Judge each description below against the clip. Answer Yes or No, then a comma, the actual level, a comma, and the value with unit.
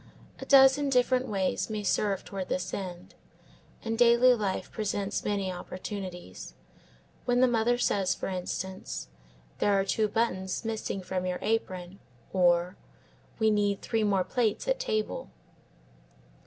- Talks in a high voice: Yes, high, 205 Hz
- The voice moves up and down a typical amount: Yes, average, 3.4 semitones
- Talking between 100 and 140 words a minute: Yes, slow, 135 wpm